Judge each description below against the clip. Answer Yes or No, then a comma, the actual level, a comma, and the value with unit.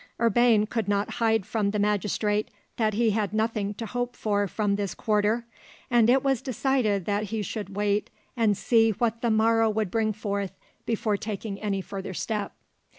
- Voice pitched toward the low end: No, high, 215 Hz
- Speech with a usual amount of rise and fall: No, narrow, 1.9 semitones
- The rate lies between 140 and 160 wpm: No, average, 175 wpm